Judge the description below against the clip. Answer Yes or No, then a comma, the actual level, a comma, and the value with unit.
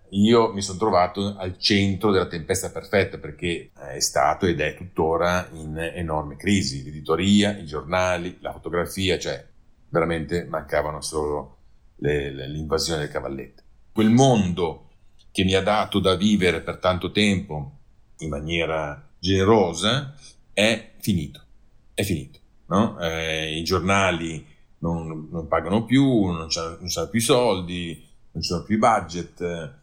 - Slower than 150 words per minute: Yes, average, 135 wpm